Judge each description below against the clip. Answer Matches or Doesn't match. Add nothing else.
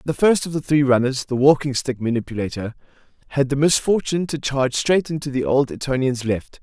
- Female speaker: Doesn't match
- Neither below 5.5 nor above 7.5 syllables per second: Matches